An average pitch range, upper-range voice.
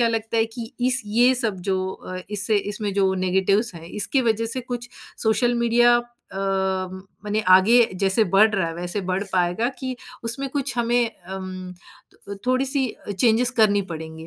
Yes: average, 4.1 semitones; high, 215 Hz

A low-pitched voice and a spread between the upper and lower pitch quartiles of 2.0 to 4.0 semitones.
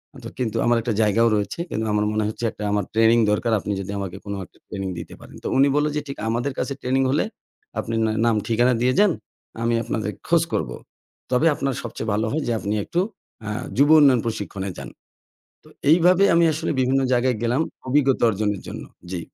No: low, 115 Hz; average, 4.4 semitones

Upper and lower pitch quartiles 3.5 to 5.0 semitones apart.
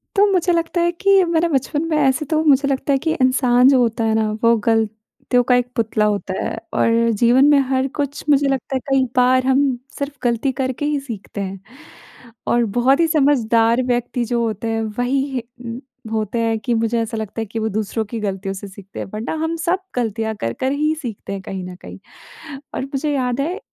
Yes: average, 4.0 semitones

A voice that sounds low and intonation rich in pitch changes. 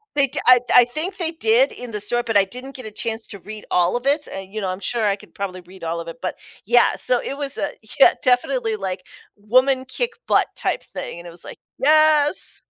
No: high, 240 Hz; wide, 5.8 semitones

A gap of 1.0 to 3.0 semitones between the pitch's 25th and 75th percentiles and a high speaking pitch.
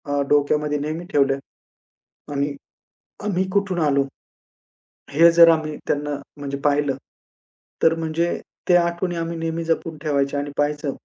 No: average, 2.7 semitones; medium, 155 Hz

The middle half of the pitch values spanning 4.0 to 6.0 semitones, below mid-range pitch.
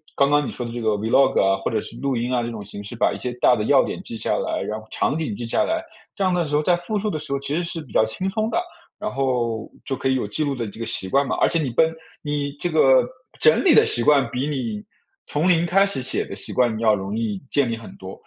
Yes: wide, 5.4 semitones; low, 130 Hz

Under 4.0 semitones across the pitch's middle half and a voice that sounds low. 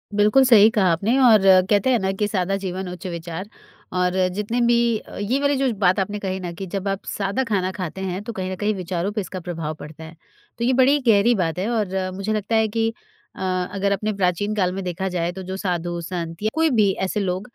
No: average, 2.9 semitones; high, 195 Hz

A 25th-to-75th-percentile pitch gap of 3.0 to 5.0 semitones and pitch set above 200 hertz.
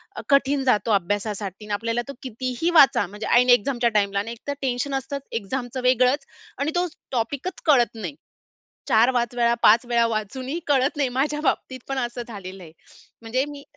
Yes: average, 3.5 semitones; high, 245 Hz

